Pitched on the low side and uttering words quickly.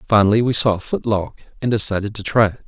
Yes: low, 105 Hz; fast, 245 wpm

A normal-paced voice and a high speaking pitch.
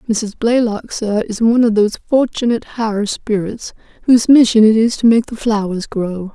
Yes: average, 180 wpm; high, 220 Hz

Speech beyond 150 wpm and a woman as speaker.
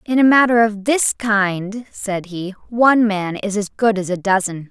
Yes: fast, 205 wpm; female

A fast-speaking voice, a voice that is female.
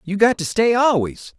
No: fast, 215 wpm; male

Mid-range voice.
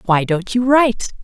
No: high, 220 Hz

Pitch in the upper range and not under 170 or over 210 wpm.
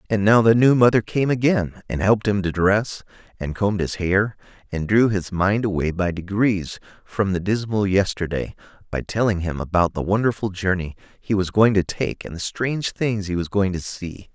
No: low, 100 Hz; average, 200 wpm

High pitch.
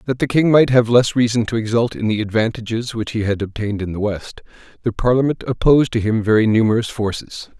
No: low, 115 Hz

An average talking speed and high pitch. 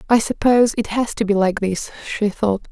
No: fast, 220 wpm; high, 210 Hz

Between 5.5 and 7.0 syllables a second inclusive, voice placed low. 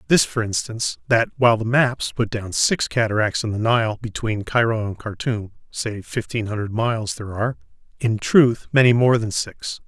No: 5.0 syllables/s; low, 110 Hz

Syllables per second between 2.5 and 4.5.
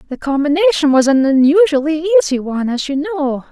No: 6.2 syllables/s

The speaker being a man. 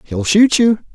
Yes: male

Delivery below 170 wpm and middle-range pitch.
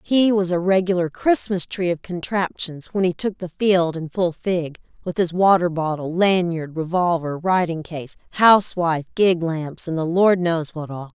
No: average, 175 wpm; medium, 175 Hz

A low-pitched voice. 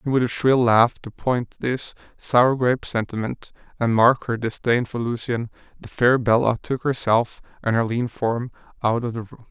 Yes: low, 120 Hz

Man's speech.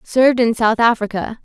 No: female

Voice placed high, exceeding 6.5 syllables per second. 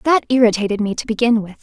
No: high, 230 Hz; 6.4 syllables/s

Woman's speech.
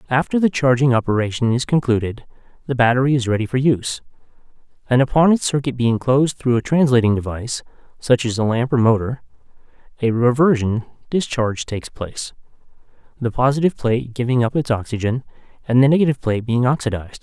No: male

